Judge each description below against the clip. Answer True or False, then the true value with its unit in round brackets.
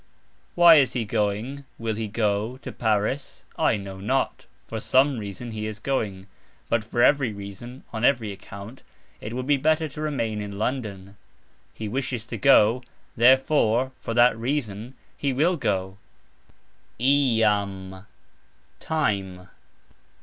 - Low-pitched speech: True (115 Hz)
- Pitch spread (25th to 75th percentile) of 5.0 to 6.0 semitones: False (4.4 semitones)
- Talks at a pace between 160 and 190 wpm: False (135 wpm)